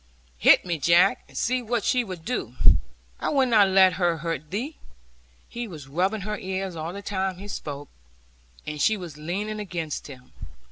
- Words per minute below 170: No, average, 180 wpm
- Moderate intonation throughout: Yes, average, 4.7 semitones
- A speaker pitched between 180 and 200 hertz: Yes, medium, 185 Hz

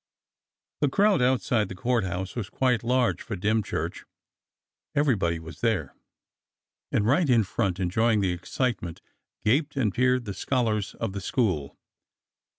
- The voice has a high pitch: No, low, 110 Hz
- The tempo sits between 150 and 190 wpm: No, average, 140 wpm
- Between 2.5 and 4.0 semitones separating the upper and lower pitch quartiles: No, average, 5.0 semitones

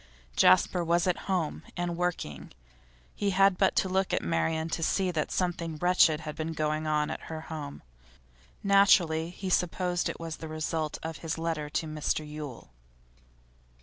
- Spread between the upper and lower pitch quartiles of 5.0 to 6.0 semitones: No, narrow, 2.5 semitones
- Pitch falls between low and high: Yes, medium, 165 Hz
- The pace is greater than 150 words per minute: Yes, average, 160 wpm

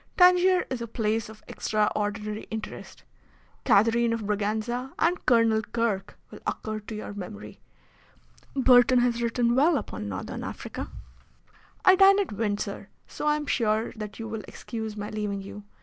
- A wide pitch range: No, average, 2.7 semitones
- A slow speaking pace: No, average, 150 wpm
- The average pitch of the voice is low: No, high, 225 Hz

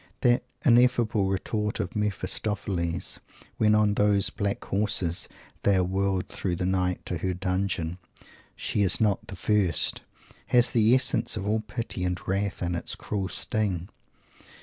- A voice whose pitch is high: No, low, 100 Hz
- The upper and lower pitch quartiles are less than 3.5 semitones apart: Yes, average, 2.7 semitones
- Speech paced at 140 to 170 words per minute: Yes, average, 150 wpm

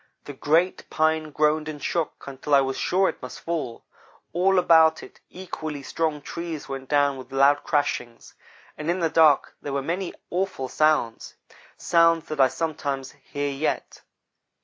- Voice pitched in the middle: Yes, medium, 155 Hz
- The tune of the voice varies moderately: Yes, average, 3.1 semitones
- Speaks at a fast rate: No, average, 160 wpm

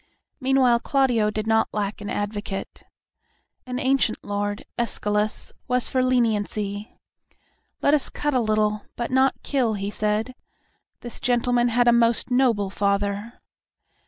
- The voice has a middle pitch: No, high, 225 Hz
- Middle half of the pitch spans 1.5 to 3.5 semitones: Yes, average, 3.2 semitones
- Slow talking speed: Yes, slow, 130 wpm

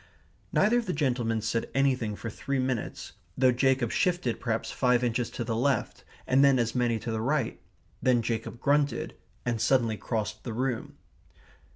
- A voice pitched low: Yes, low, 125 Hz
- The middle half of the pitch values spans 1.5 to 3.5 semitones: Yes, average, 2.8 semitones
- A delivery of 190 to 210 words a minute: No, average, 170 wpm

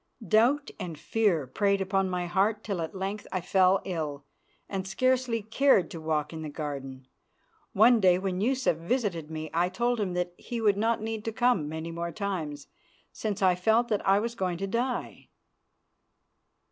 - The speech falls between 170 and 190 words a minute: Yes, average, 175 wpm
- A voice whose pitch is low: No, high, 190 Hz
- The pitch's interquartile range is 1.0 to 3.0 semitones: No, average, 4.8 semitones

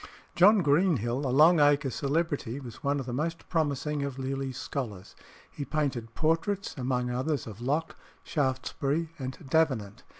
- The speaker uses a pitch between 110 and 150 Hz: Yes, medium, 140 Hz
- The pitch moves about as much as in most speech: Yes, average, 3.6 semitones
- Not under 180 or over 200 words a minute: No, average, 145 wpm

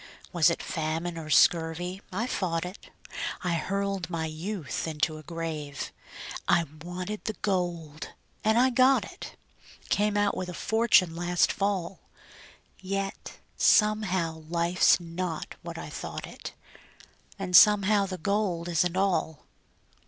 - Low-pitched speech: No, medium, 180 Hz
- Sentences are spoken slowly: Yes, slow, 130 wpm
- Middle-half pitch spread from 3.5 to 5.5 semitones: No, average, 3.1 semitones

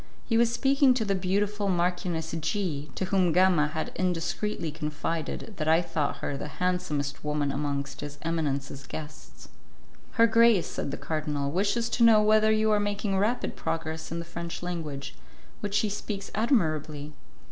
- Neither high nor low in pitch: Yes, medium, 175 Hz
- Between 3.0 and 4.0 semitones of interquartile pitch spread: No, average, 5.3 semitones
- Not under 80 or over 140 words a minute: No, average, 160 wpm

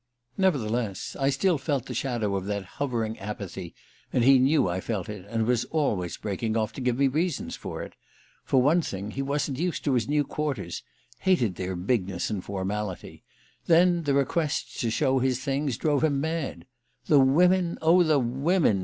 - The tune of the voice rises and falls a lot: Yes, wide, 5.9 semitones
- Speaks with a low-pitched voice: Yes, low, 130 Hz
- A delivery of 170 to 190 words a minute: Yes, average, 180 wpm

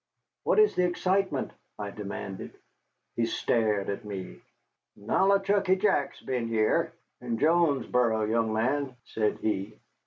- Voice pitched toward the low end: Yes, low, 115 Hz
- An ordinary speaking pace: No, slow, 120 wpm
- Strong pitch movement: Yes, wide, 8.1 semitones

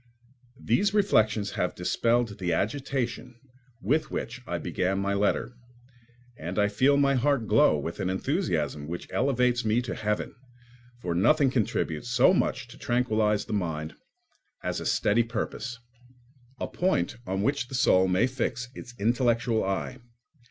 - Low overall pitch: Yes, low, 115 Hz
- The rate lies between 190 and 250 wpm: No, average, 145 wpm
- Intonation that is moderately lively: Yes, average, 4.4 semitones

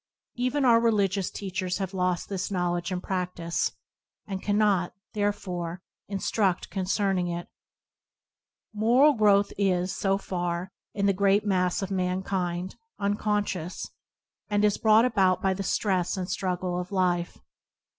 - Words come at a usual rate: No, slow, 130 wpm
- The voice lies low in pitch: No, high, 190 Hz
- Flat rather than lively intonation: Yes, narrow, 2.2 semitones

